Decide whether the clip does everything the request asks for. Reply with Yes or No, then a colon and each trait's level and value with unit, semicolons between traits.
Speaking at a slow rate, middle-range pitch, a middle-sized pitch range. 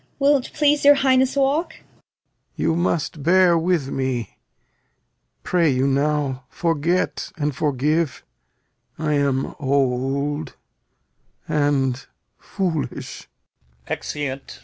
Yes: slow, 100 wpm; medium, 150 Hz; average, 4.8 semitones